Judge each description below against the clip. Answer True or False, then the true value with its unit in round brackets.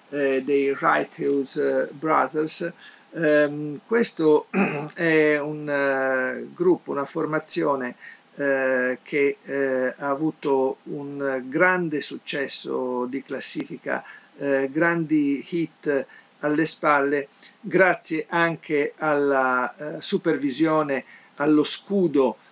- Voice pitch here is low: False (150 Hz)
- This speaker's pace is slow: True (95 wpm)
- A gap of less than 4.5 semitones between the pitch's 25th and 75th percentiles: True (2.7 semitones)